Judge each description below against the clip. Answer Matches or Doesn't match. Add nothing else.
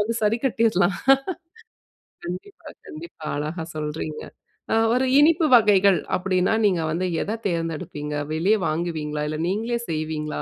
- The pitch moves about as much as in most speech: Doesn't match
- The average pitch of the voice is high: Doesn't match